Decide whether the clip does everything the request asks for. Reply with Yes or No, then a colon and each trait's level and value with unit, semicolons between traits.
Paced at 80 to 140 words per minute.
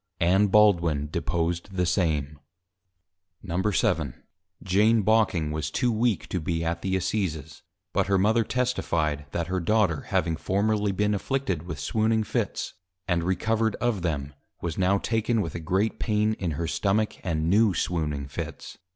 No: average, 150 wpm